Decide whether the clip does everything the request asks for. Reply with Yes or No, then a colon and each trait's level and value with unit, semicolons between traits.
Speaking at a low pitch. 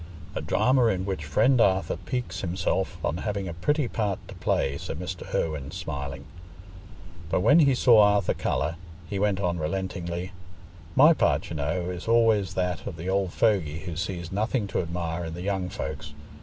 Yes: very low, 95 Hz